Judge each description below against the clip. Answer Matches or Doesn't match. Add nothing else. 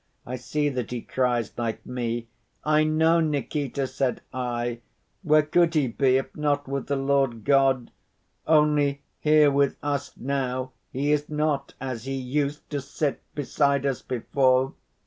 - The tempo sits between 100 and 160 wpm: Matches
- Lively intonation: Doesn't match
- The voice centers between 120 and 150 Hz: Matches